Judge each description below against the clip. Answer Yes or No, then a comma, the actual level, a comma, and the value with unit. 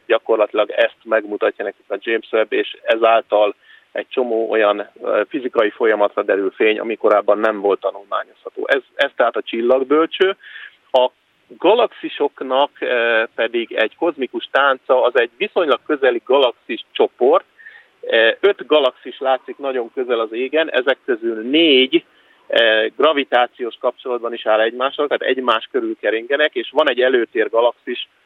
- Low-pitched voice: No, very high, 390 Hz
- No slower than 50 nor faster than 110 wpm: No, average, 130 wpm